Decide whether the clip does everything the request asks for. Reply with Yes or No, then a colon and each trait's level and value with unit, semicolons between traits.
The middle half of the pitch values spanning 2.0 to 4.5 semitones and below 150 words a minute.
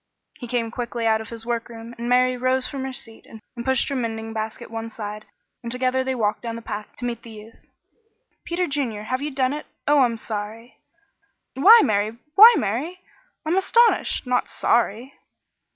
No: average, 2.8 semitones; average, 185 wpm